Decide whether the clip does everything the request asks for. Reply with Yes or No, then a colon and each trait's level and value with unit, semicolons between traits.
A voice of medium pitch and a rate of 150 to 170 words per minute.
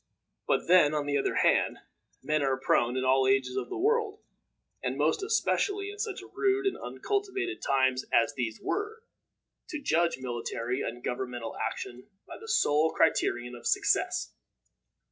Yes: medium, 145 Hz; average, 155 wpm